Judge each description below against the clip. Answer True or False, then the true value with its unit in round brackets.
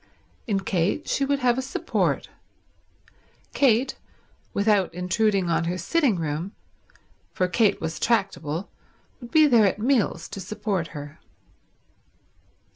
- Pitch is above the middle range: True (200 Hz)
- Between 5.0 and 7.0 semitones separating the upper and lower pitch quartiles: True (5.3 semitones)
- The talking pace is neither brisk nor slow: False (120 wpm)